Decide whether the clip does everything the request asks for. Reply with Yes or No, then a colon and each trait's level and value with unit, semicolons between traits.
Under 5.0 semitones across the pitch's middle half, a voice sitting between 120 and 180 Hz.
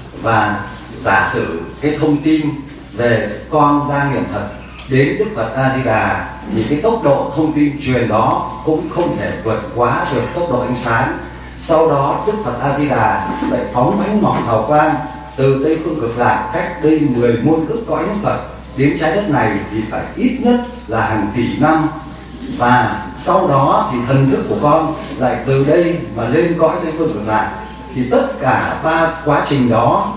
No: wide, 5.5 semitones; low, 135 Hz